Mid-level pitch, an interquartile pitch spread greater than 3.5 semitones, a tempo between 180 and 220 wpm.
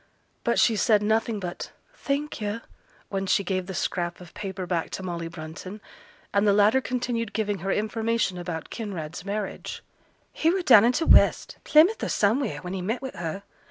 No: high, 205 Hz; average, 4.1 semitones; average, 185 wpm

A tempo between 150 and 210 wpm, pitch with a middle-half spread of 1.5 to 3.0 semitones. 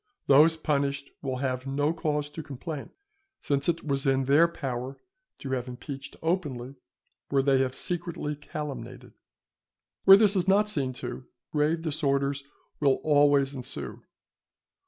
No: slow, 135 wpm; narrow, 2.6 semitones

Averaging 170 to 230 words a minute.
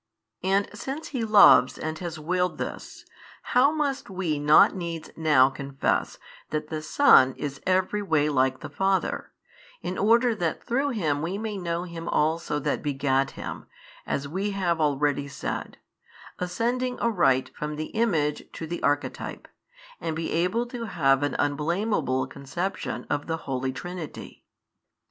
No: average, 150 wpm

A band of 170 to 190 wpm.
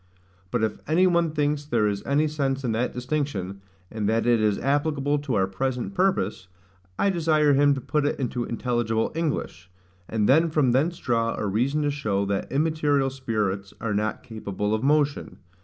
Yes: average, 180 wpm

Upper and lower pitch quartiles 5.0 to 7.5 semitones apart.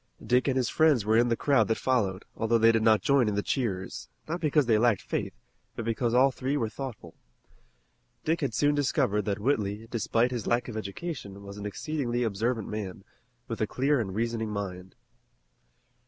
No: average, 3.9 semitones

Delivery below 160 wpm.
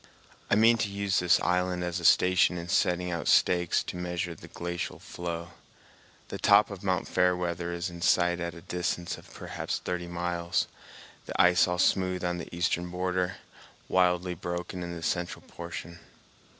No: average, 170 wpm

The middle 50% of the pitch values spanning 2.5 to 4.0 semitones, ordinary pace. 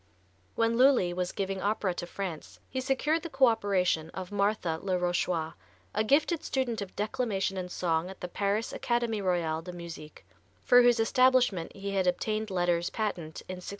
No: average, 4.4 semitones; average, 175 wpm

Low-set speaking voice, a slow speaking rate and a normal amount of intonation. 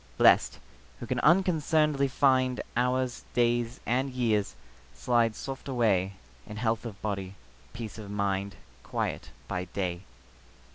Yes: low, 120 Hz; slow, 125 wpm; average, 4.3 semitones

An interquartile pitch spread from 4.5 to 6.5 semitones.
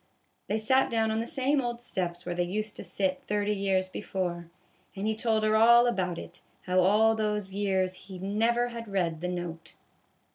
No: average, 3.2 semitones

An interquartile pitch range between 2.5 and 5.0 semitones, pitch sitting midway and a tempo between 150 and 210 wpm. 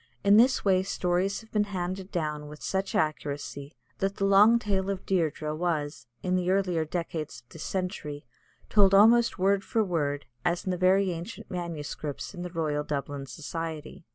Yes: average, 4.3 semitones; medium, 180 Hz; average, 175 wpm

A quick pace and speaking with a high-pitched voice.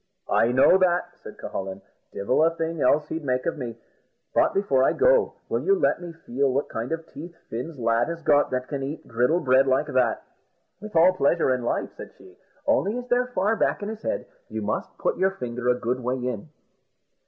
No: fast, 210 wpm; medium, 145 Hz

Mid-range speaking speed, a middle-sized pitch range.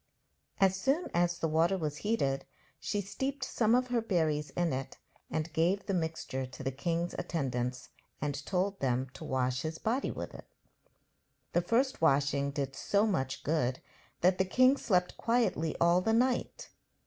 No: average, 165 wpm; wide, 6.6 semitones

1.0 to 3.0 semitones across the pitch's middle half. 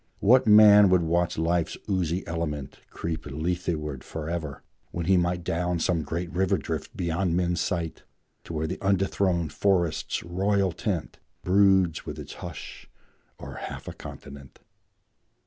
Yes: narrow, 2.6 semitones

